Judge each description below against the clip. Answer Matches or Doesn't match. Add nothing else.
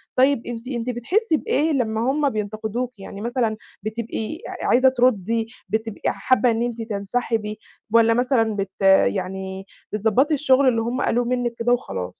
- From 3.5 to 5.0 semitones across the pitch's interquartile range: Doesn't match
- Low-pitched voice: Doesn't match